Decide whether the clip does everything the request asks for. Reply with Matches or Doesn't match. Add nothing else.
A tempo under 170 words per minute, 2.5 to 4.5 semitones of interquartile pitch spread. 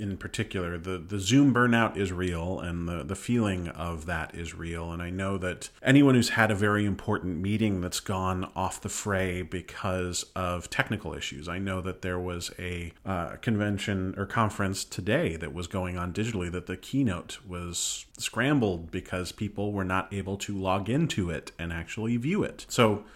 Doesn't match